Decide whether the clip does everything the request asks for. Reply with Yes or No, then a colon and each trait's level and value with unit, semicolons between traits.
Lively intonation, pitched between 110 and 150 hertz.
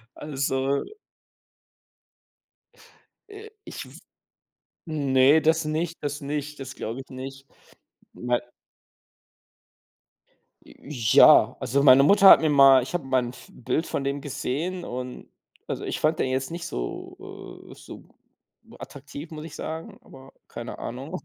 No: average, 3.0 semitones; medium, 140 Hz